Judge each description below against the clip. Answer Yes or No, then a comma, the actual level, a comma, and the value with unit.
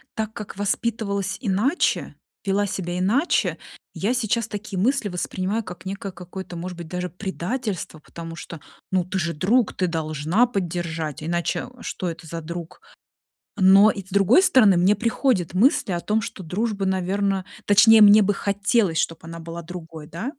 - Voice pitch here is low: No, high, 190 Hz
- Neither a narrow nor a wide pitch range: Yes, average, 3.5 semitones